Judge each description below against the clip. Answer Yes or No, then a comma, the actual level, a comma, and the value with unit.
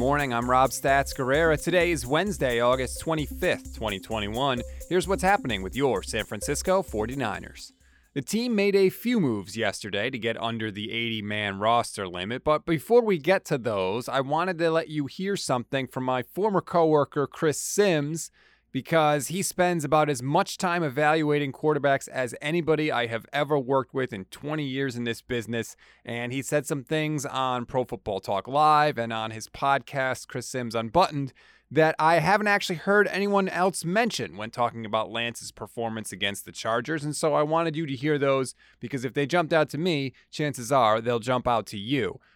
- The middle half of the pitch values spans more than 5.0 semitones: Yes, wide, 5.5 semitones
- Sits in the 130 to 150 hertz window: Yes, medium, 140 Hz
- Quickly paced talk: No, average, 185 wpm